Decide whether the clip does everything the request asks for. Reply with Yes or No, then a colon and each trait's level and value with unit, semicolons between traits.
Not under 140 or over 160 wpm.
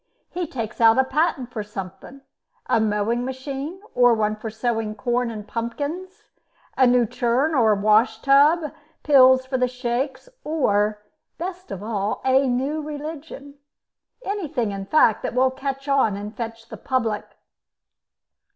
Yes: average, 145 wpm